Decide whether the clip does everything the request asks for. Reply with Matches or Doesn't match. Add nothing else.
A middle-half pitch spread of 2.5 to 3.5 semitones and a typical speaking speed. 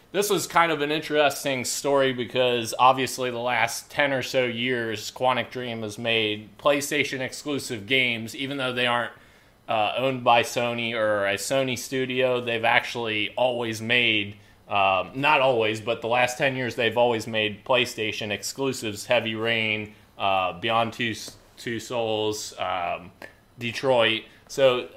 Matches